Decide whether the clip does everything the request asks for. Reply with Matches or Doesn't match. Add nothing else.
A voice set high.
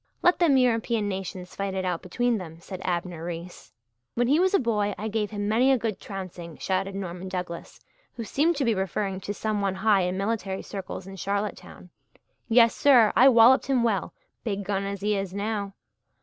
Matches